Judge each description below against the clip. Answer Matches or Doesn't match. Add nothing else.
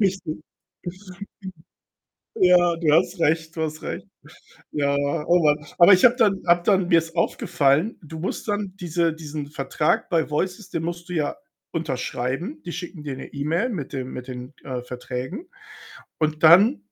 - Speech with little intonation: Doesn't match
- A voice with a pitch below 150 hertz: Doesn't match